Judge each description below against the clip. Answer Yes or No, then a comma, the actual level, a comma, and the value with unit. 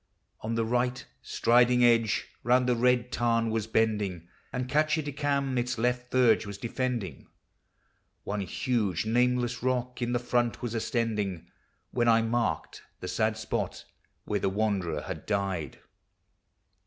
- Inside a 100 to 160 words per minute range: Yes, average, 140 wpm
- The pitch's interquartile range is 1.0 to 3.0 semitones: Yes, average, 2.7 semitones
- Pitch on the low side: Yes, low, 115 Hz